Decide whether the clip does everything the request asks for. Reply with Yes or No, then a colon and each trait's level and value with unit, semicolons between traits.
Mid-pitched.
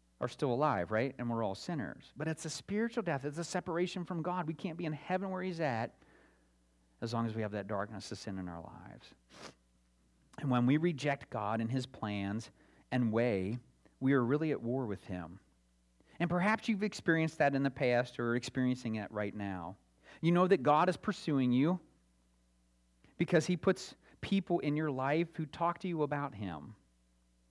No: low, 125 Hz